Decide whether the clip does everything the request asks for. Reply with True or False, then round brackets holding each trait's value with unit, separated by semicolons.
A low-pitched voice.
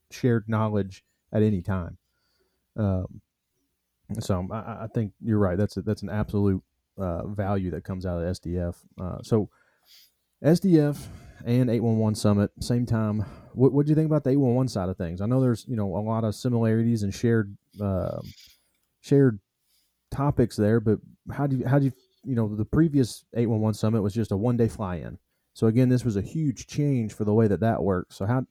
True (110 Hz)